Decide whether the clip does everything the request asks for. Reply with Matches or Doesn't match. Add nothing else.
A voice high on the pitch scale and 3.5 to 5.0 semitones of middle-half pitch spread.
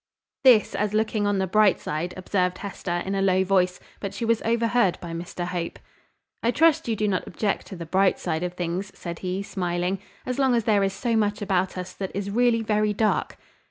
Doesn't match